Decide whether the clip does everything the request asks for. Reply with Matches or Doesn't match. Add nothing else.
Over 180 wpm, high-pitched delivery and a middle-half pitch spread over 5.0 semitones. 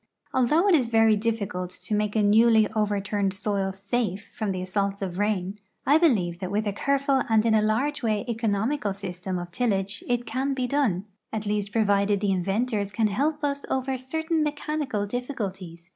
Doesn't match